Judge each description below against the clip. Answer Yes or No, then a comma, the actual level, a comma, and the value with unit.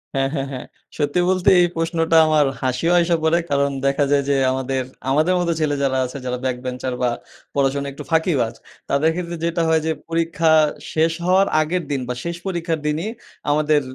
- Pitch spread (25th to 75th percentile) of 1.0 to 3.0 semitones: No, average, 3.5 semitones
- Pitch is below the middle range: No, medium, 155 Hz